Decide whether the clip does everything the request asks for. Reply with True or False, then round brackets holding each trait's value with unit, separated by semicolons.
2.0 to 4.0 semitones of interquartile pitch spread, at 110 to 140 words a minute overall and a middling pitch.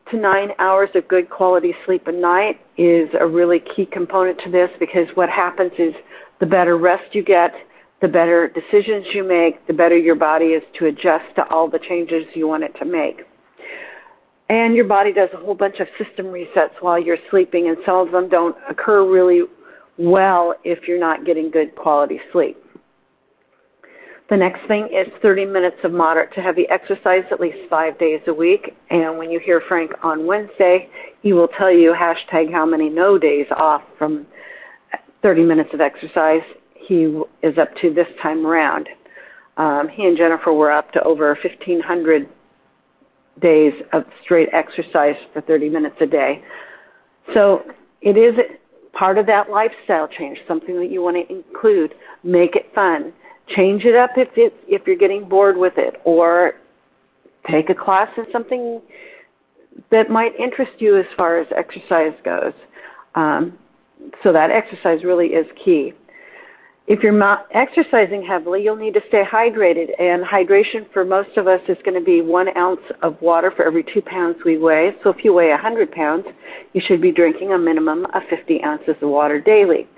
False (3.7 semitones; 175 wpm; 180 Hz)